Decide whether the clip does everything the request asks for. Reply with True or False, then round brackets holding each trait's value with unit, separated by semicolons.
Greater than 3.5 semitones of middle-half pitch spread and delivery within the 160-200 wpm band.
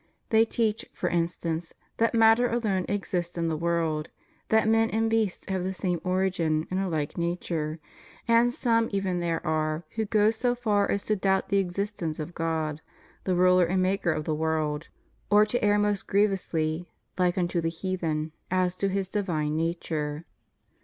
True (4.0 semitones; 175 wpm)